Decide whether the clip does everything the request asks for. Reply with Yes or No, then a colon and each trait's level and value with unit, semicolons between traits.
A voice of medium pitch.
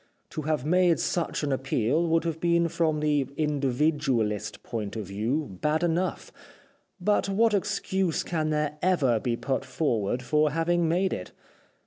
Yes: medium, 150 Hz